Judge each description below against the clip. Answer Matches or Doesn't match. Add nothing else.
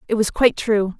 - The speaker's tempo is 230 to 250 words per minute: Matches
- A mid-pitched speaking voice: Doesn't match